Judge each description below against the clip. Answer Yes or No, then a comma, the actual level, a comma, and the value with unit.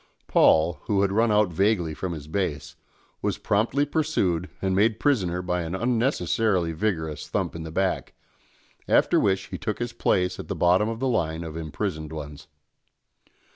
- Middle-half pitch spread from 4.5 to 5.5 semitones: Yes, average, 5.0 semitones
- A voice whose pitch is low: Yes, very low, 95 Hz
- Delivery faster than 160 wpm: Yes, average, 170 wpm